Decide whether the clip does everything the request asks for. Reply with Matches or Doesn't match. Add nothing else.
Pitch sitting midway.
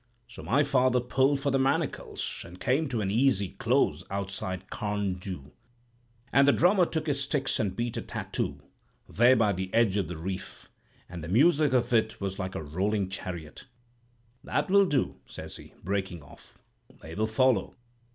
Doesn't match